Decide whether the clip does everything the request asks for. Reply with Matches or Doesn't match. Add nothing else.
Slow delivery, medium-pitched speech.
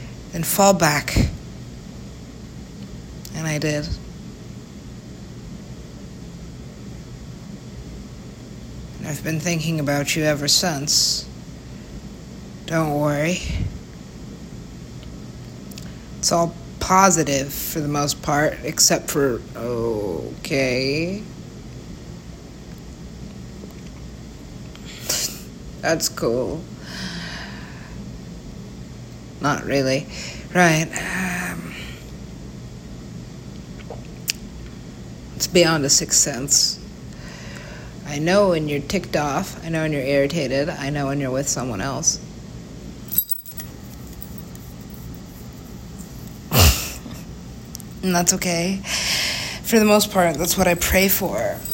Matches